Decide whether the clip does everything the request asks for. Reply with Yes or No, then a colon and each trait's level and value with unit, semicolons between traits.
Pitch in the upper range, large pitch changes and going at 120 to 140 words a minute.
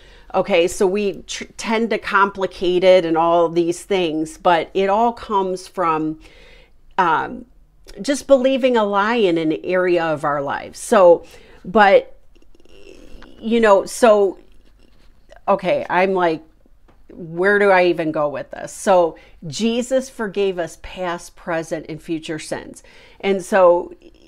Yes: high, 195 Hz; wide, 6.3 semitones; slow, 135 wpm